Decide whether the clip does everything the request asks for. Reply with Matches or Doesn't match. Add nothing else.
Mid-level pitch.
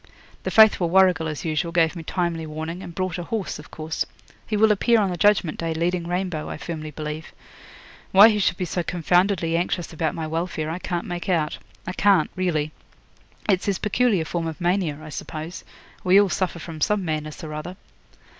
Matches